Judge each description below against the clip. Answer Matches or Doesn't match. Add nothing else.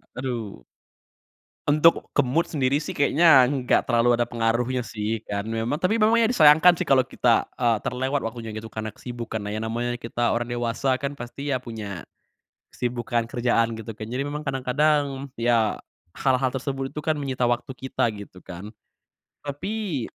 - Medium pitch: Doesn't match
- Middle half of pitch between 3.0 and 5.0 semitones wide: Matches